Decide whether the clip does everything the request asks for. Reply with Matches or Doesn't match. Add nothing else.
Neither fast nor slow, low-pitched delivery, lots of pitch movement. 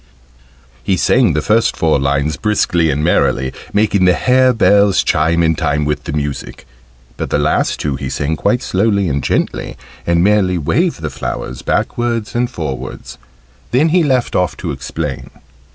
Matches